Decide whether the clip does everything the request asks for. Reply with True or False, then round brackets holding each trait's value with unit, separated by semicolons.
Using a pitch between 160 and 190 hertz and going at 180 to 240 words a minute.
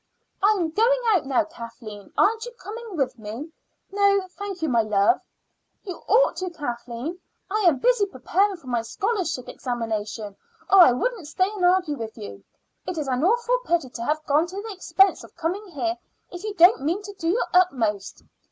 False (345 Hz; 190 wpm)